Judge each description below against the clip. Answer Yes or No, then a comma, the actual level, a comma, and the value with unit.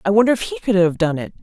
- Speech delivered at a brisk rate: Yes, fast, 335 wpm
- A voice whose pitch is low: No, high, 190 Hz